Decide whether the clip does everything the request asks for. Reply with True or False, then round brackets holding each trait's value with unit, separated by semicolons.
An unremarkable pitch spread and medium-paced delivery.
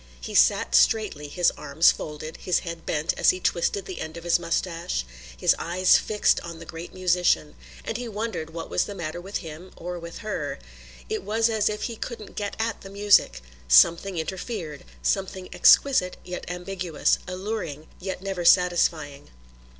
True (3.4 semitones; 170 wpm)